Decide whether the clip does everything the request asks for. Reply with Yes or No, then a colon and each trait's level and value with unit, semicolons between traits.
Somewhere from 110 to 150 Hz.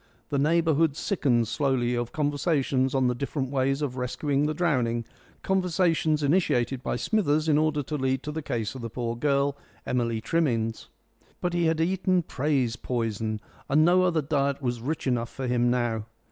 Yes: medium, 140 Hz